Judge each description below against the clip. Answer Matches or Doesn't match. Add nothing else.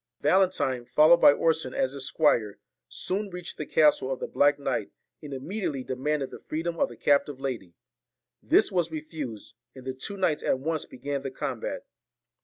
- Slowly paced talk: Doesn't match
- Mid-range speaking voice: Matches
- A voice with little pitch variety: Doesn't match